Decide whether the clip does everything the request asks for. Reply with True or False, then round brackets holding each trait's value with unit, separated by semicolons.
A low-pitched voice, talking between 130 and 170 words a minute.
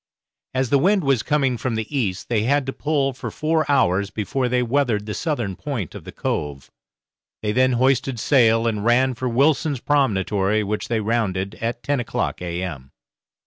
False (120 Hz; 180 wpm)